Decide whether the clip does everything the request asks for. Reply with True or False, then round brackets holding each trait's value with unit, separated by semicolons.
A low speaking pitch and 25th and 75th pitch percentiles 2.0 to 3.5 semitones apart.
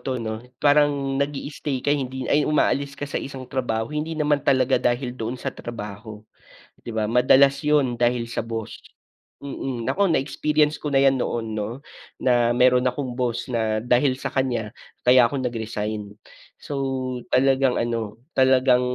True (125 Hz; 3.0 semitones)